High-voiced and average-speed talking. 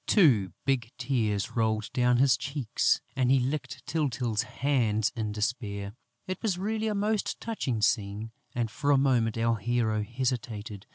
No: low, 120 Hz; average, 155 wpm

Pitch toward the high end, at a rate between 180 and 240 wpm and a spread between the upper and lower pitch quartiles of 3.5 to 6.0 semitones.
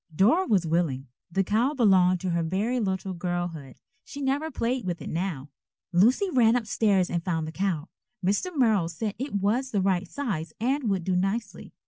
Yes: high, 195 Hz; average, 185 wpm; average, 5.0 semitones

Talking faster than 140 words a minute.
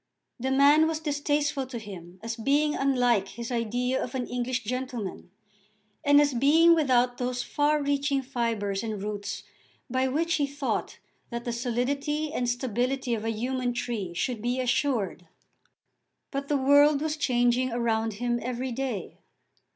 Yes: average, 150 wpm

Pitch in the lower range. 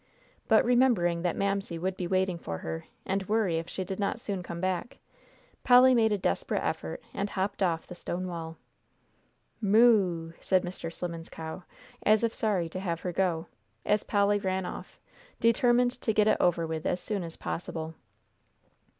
No: medium, 185 Hz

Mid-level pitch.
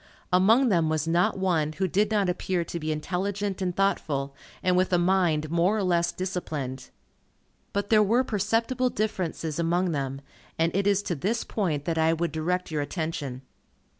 Yes: medium, 180 Hz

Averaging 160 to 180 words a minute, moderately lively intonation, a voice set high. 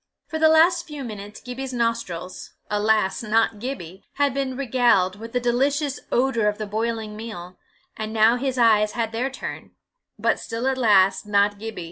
Yes: average, 165 wpm; average, 3.8 semitones; high, 230 Hz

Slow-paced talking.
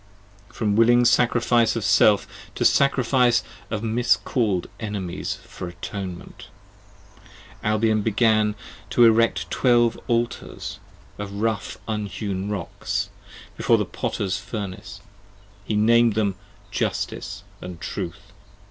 Yes: slow, 105 wpm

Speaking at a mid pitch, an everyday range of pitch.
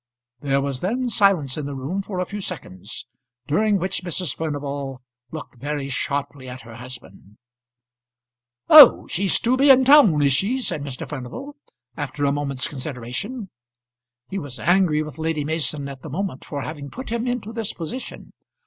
No: medium, 150 Hz; wide, 6.3 semitones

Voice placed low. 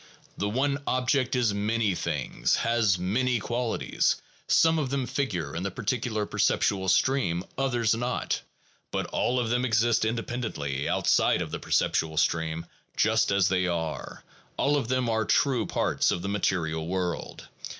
Yes: low, 110 Hz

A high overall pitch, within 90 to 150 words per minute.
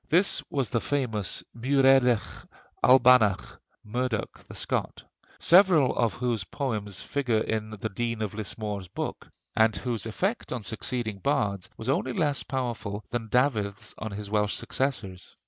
No: low, 115 Hz; average, 140 wpm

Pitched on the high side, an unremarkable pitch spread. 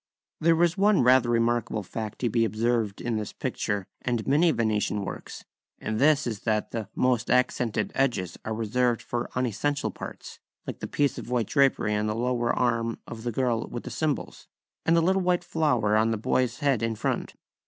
No: low, 120 Hz; average, 3.5 semitones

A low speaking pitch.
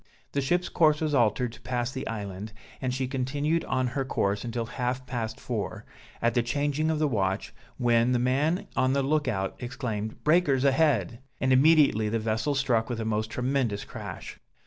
Yes: low, 125 Hz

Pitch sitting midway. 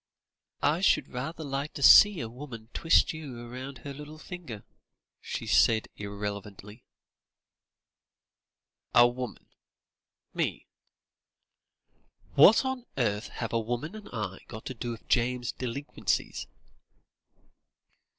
No: low, 125 Hz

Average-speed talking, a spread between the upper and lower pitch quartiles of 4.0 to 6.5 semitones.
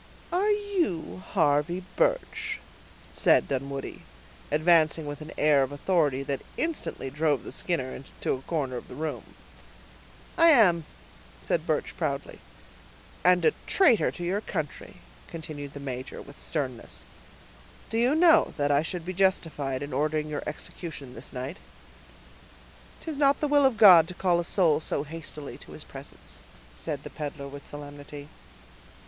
Yes: average, 150 wpm; average, 4.6 semitones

